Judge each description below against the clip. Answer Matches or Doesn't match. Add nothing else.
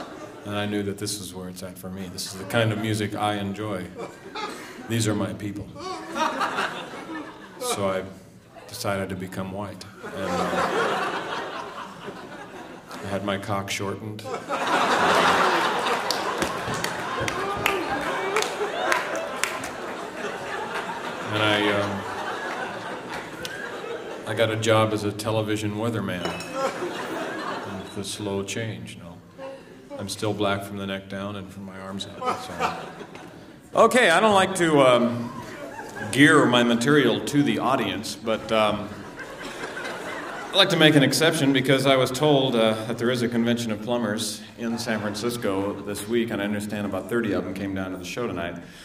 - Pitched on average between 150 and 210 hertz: Doesn't match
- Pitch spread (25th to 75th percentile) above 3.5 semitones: Doesn't match